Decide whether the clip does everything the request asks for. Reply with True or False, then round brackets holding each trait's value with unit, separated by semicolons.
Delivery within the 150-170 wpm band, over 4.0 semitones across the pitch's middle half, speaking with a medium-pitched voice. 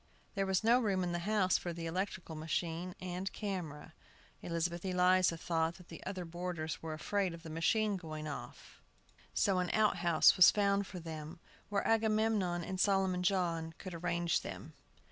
False (165 wpm; 2.8 semitones; 180 Hz)